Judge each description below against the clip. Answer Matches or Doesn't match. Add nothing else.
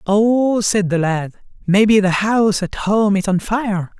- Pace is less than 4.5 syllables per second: Matches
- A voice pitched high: Matches